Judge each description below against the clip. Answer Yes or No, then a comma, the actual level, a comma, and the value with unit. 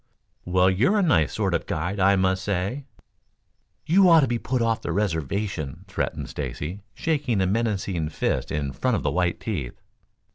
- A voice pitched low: Yes, very low, 95 Hz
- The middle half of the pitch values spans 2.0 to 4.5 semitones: No, average, 5.1 semitones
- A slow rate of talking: No, average, 180 wpm